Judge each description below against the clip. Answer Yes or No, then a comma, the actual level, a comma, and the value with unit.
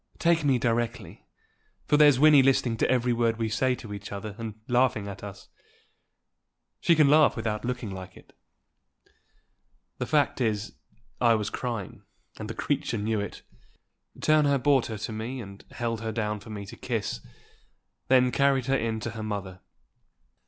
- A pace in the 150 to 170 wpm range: Yes, average, 165 wpm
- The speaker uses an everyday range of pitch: Yes, average, 3.6 semitones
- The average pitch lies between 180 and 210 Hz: No, low, 115 Hz